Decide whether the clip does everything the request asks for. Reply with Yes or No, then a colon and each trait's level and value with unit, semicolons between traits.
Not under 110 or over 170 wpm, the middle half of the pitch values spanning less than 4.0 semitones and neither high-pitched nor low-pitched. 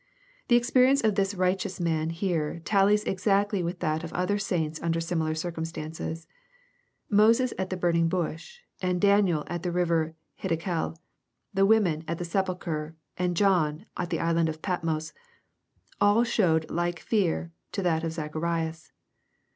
Yes: average, 160 wpm; average, 3.2 semitones; medium, 175 Hz